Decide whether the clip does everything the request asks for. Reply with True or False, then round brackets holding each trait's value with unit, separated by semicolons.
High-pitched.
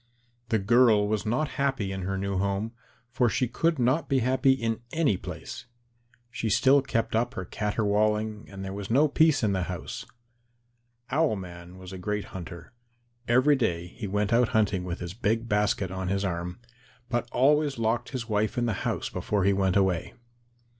False (105 Hz)